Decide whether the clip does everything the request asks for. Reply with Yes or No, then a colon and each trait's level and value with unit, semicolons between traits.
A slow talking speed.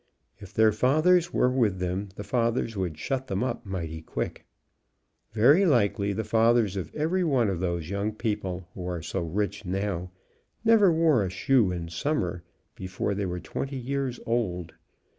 No: average, 165 wpm